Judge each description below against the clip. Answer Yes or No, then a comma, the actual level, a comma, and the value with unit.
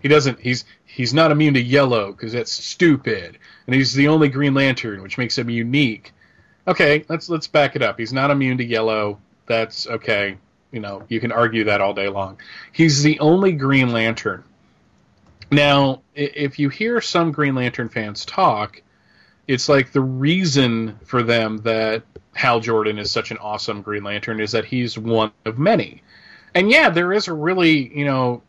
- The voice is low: Yes, low, 125 Hz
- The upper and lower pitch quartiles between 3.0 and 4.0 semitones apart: No, average, 4.6 semitones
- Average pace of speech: Yes, average, 180 wpm